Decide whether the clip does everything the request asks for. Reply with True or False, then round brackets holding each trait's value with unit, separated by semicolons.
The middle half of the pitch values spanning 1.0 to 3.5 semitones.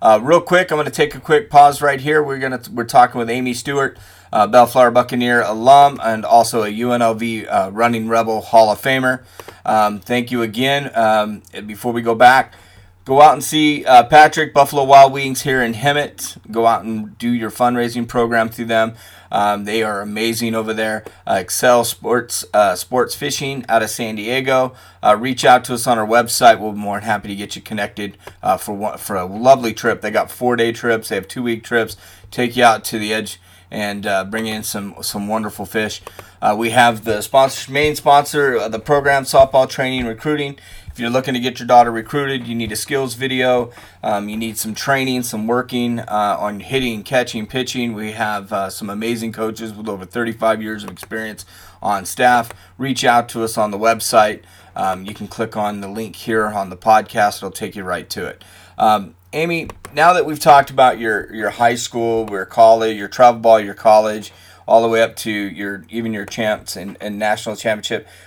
True (3.0 semitones)